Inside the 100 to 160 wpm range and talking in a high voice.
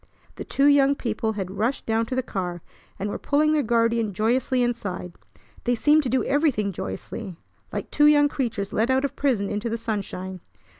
No: average, 190 wpm; high, 230 Hz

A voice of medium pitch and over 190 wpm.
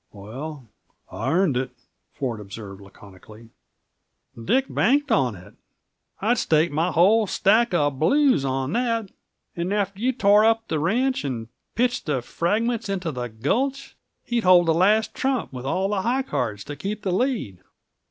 No: medium, 180 Hz; average, 155 wpm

